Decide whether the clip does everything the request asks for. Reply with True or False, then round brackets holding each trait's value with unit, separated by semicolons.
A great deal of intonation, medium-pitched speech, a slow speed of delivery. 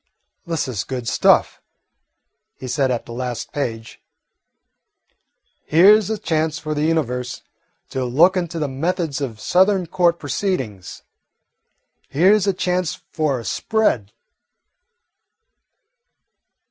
True (6.3 semitones; 155 Hz; 120 wpm)